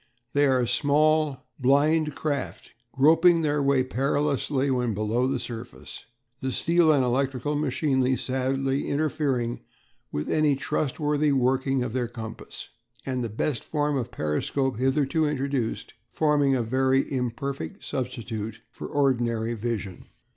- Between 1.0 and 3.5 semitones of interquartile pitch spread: Yes, average, 2.9 semitones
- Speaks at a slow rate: Yes, slow, 125 wpm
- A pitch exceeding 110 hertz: Yes, low, 135 Hz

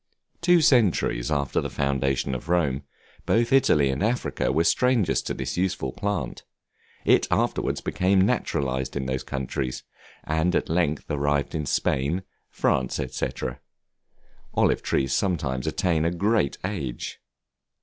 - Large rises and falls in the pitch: Yes, wide, 6.1 semitones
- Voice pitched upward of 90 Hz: No, very low, 75 Hz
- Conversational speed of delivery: No, slow, 130 wpm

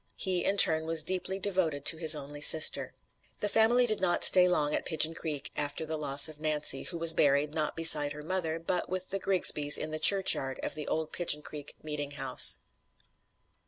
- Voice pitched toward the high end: No, medium, 160 Hz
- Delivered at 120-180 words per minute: No, average, 195 wpm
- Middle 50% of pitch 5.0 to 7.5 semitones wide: No, average, 3.5 semitones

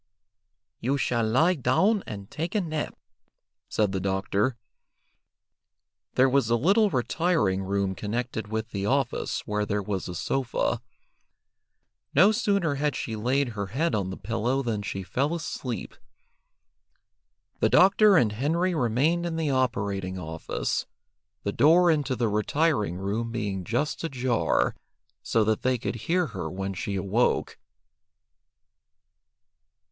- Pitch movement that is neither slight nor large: No, wide, 6.8 semitones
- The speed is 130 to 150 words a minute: Yes, slow, 135 wpm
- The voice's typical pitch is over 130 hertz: No, low, 120 Hz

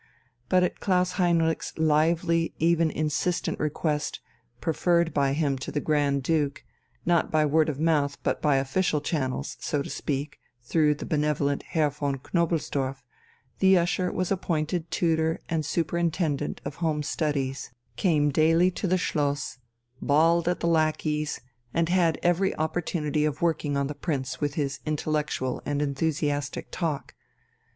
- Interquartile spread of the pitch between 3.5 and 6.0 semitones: No, narrow, 2.6 semitones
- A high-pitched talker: No, medium, 155 Hz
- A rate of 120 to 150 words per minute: Yes, average, 145 wpm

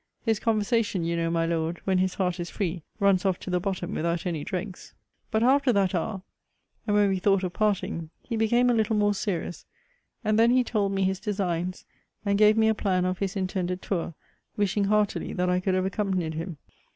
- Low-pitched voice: No, high, 190 Hz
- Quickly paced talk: Yes, fast, 210 wpm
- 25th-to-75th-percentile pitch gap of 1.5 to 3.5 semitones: Yes, average, 2.8 semitones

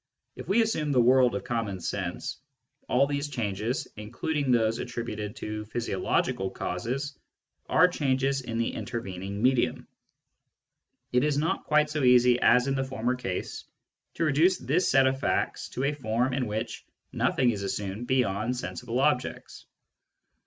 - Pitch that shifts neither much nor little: Yes, average, 3.9 semitones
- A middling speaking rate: Yes, average, 150 wpm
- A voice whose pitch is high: No, low, 125 Hz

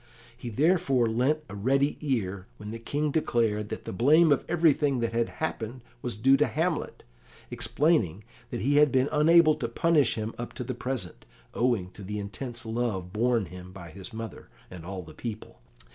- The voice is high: No, low, 120 Hz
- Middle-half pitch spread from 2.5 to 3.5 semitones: No, wide, 5.4 semitones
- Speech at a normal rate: Yes, average, 185 wpm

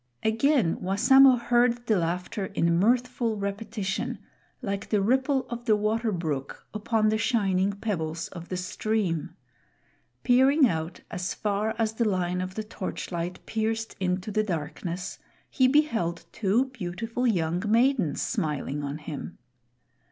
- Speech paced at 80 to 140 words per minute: Yes, slow, 135 wpm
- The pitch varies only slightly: No, average, 4.5 semitones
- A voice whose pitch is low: No, high, 210 Hz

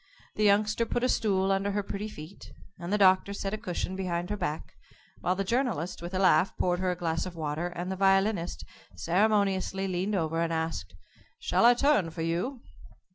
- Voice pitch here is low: No, high, 190 Hz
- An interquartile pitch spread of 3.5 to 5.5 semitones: No, average, 3.0 semitones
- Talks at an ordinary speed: Yes, average, 195 wpm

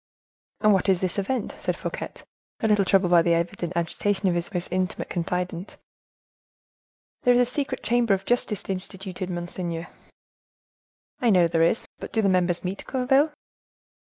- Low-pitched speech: No, high, 190 Hz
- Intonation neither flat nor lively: Yes, average, 3.4 semitones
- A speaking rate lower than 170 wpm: Yes, average, 160 wpm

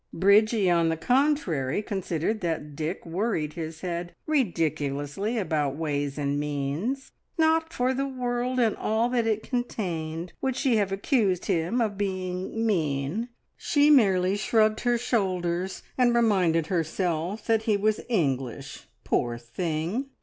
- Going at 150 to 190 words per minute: No, slow, 135 wpm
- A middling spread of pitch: No, wide, 6.3 semitones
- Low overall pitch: No, high, 190 Hz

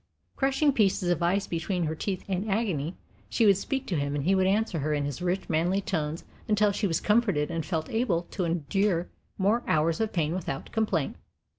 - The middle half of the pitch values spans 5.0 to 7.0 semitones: No, average, 4.3 semitones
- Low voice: No, medium, 185 Hz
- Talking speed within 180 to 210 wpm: Yes, average, 200 wpm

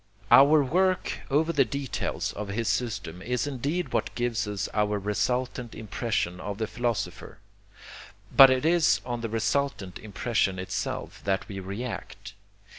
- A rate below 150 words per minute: Yes, average, 140 wpm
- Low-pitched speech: Yes, low, 115 Hz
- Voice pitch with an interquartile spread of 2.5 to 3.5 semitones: No, average, 4.7 semitones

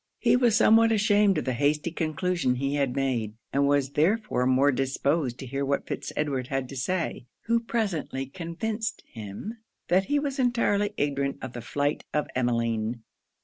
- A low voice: No, medium, 145 Hz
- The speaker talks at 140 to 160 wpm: No, average, 170 wpm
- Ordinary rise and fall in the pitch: No, wide, 7.8 semitones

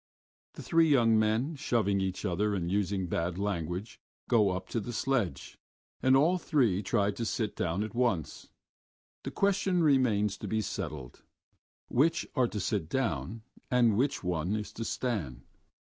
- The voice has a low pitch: Yes, low, 105 Hz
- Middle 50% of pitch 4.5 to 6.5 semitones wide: Yes, average, 5.1 semitones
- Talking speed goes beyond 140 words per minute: Yes, average, 160 wpm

